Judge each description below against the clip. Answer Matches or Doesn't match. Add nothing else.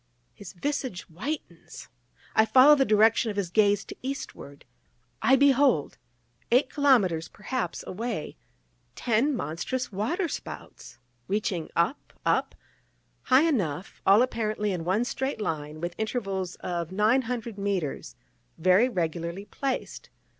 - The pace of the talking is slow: Matches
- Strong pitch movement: Matches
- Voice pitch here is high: Matches